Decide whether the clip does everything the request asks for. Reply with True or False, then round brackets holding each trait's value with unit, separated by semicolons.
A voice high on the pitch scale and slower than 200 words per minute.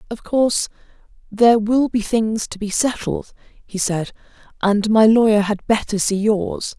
True (215 Hz; 160 wpm)